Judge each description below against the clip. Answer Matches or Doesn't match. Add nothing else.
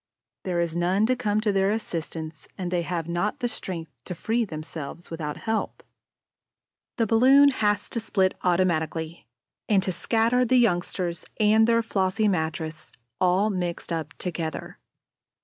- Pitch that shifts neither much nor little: Matches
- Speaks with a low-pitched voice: Doesn't match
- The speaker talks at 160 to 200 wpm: Doesn't match